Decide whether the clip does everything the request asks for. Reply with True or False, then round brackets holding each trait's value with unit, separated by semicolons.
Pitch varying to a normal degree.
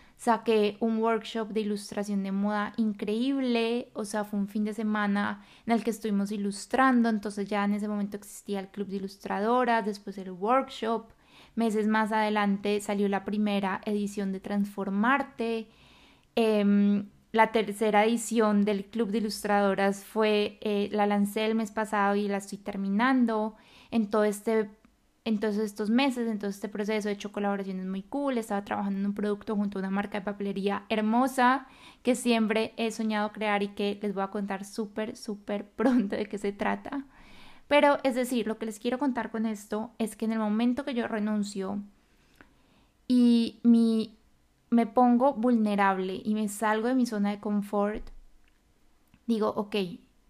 False (1.9 semitones)